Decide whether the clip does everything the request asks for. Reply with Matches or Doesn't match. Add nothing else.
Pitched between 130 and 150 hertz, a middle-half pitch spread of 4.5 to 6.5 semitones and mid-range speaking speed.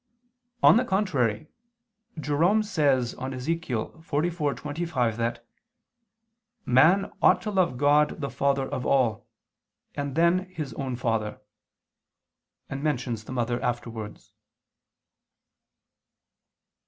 Doesn't match